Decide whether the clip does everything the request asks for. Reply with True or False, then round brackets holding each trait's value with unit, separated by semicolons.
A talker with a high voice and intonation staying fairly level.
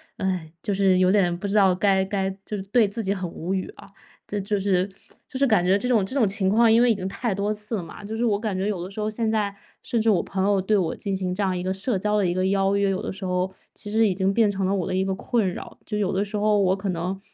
True (195 Hz; 2.0 semitones)